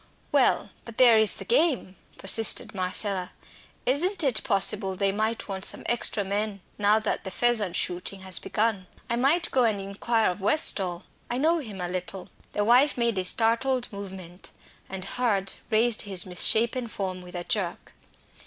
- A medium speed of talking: Yes, average, 165 wpm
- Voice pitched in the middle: No, high, 210 Hz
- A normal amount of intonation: Yes, average, 3.9 semitones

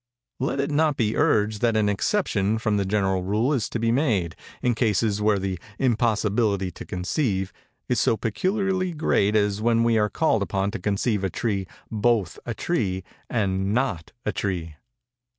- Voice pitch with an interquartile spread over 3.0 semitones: Yes, average, 3.4 semitones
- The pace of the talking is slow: No, average, 170 wpm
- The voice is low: Yes, low, 105 Hz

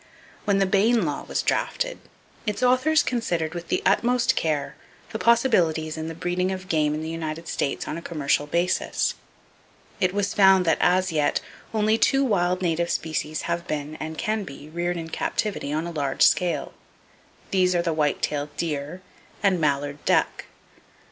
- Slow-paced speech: No, average, 170 wpm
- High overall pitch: No, medium, 170 Hz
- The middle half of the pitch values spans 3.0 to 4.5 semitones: Yes, average, 4.0 semitones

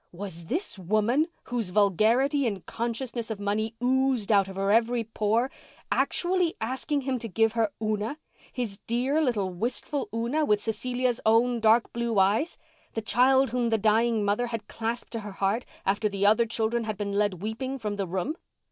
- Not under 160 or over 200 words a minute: Yes, average, 175 wpm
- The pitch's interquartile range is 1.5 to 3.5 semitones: Yes, average, 3.1 semitones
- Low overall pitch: No, high, 225 Hz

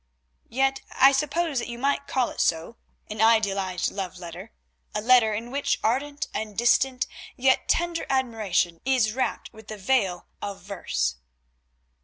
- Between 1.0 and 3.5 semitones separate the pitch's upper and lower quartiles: No, average, 5.2 semitones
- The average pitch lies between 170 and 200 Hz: No, high, 230 Hz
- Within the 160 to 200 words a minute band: No, average, 150 wpm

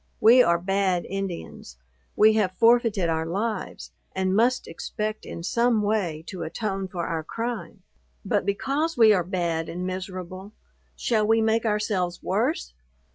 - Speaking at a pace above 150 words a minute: No, average, 145 wpm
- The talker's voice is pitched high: Yes, high, 195 Hz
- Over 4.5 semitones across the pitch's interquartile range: No, average, 3.9 semitones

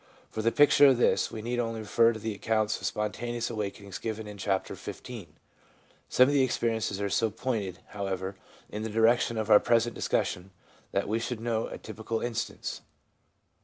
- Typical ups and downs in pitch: No, narrow, 2.1 semitones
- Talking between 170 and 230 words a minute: Yes, average, 180 wpm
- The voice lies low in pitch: Yes, low, 110 Hz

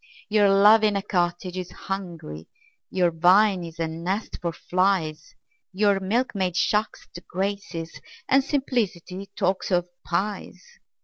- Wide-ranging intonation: No, average, 3.0 semitones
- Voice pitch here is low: No, high, 190 Hz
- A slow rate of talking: Yes, slow, 130 wpm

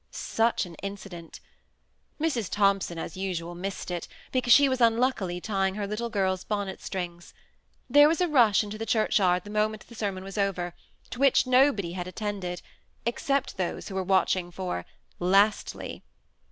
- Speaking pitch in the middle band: No, high, 200 Hz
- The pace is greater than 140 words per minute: Yes, average, 170 wpm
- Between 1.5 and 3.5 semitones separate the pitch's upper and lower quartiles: No, average, 3.9 semitones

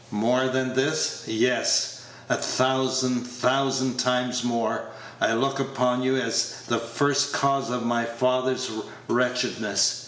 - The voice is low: Yes, low, 125 Hz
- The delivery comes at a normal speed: No, slow, 125 wpm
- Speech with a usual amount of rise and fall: No, narrow, 1.4 semitones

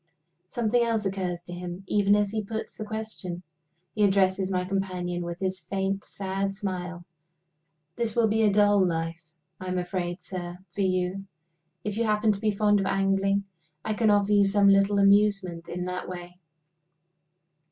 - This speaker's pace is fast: No, average, 170 wpm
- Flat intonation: Yes, narrow, 2.3 semitones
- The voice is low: No, high, 195 Hz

